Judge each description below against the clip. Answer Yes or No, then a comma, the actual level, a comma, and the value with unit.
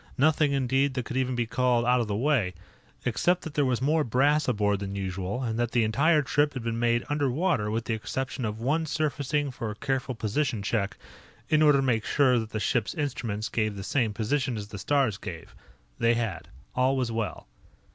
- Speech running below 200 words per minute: No, fast, 205 wpm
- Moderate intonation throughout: Yes, average, 4.3 semitones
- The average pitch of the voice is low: Yes, low, 125 Hz